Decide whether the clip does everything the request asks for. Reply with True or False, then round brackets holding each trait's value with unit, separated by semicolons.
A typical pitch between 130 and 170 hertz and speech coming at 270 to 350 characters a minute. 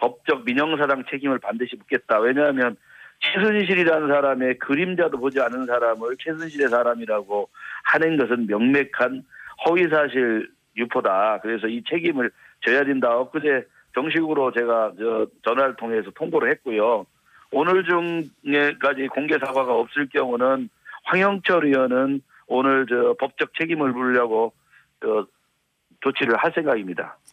True (135 Hz; 295 characters per minute)